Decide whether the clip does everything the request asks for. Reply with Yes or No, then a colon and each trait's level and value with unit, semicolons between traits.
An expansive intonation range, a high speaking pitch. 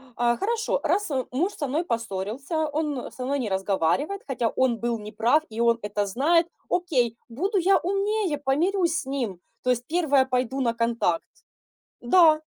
Yes: wide, 6.1 semitones; very high, 270 Hz